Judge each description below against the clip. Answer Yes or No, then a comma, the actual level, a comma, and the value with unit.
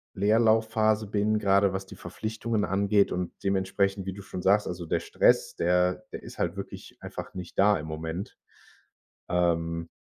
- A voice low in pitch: Yes, very low, 95 Hz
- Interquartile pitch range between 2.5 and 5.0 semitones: Yes, average, 2.8 semitones